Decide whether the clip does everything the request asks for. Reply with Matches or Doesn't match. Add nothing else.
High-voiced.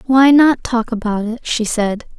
Matches